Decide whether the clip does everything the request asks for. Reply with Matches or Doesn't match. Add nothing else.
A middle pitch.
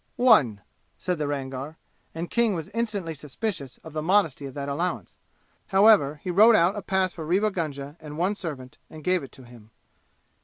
Matches